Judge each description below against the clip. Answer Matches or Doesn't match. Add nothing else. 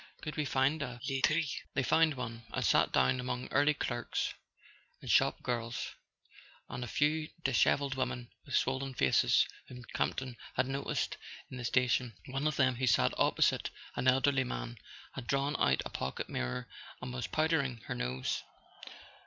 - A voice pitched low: Matches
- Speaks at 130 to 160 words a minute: Doesn't match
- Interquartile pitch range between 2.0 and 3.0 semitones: Matches